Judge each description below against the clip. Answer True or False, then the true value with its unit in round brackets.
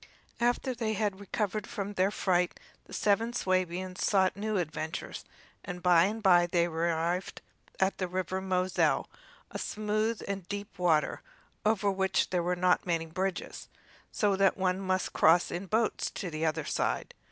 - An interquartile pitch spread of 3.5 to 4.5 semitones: False (2.4 semitones)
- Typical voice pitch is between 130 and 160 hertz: False (185 Hz)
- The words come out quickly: False (160 wpm)